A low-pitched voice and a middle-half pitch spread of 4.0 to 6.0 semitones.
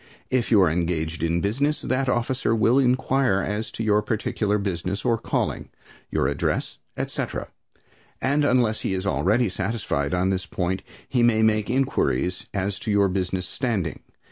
Yes: low, 105 Hz; average, 4.5 semitones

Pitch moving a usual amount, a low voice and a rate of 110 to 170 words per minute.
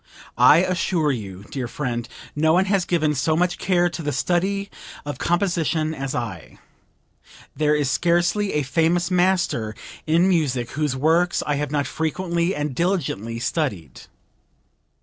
No: average, 4.5 semitones; medium, 155 Hz; average, 145 wpm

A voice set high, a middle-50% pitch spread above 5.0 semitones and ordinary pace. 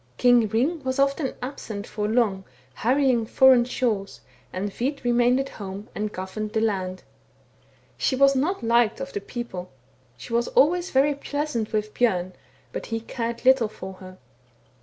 No: high, 235 Hz; average, 4.1 semitones; average, 160 wpm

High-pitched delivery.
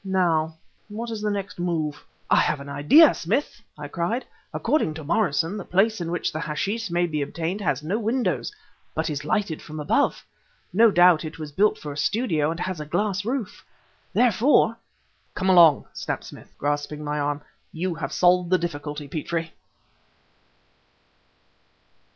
No: medium, 170 Hz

